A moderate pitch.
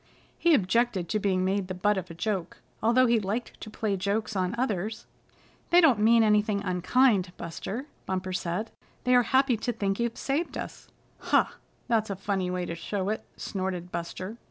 No: high, 205 Hz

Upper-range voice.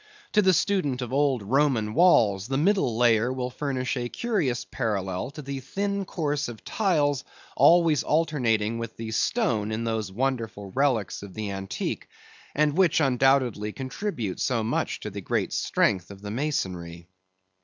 No: low, 125 Hz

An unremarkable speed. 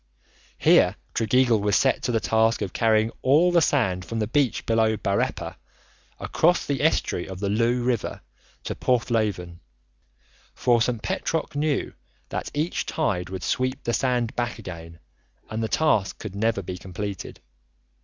Yes: average, 155 wpm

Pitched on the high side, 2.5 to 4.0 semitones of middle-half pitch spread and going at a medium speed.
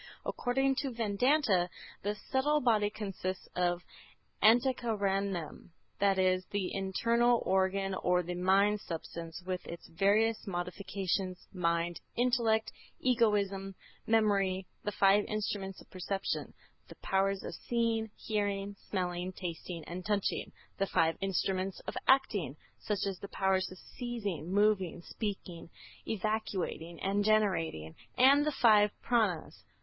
No: high, 195 Hz; average, 2.9 semitones; slow, 120 wpm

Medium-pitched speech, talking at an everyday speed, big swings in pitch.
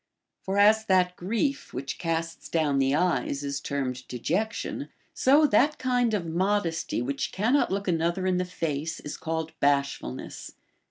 Yes: medium, 170 Hz; average, 150 wpm; wide, 6.3 semitones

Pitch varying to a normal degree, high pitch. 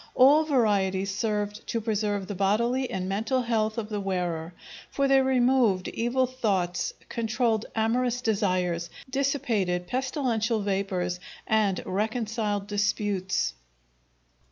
Yes: average, 4.0 semitones; high, 215 Hz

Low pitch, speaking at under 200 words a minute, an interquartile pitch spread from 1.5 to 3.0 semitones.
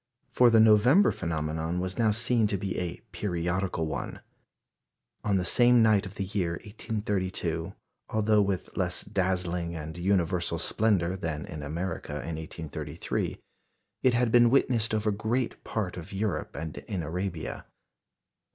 No: very low, 95 Hz; average, 140 wpm; average, 4.5 semitones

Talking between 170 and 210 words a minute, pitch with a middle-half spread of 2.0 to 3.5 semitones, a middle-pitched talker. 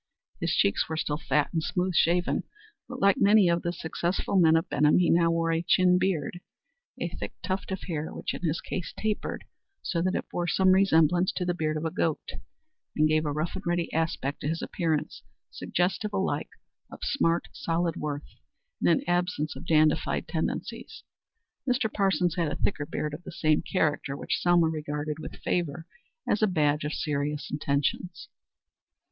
Yes: average, 180 wpm; average, 2.8 semitones; medium, 165 Hz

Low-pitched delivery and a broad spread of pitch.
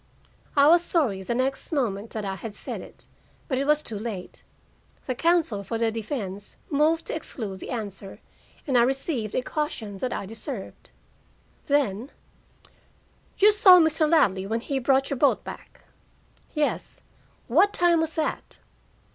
No: very high, 260 Hz; wide, 6.1 semitones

